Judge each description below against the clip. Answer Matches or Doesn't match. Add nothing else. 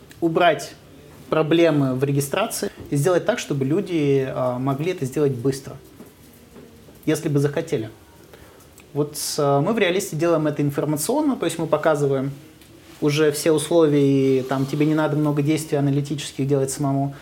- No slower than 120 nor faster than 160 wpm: Matches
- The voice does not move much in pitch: Matches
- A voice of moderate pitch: Matches